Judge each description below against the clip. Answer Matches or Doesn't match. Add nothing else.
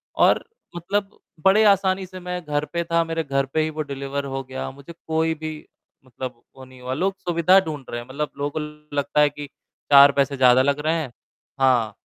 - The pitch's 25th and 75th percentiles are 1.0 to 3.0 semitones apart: Doesn't match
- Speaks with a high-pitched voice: Doesn't match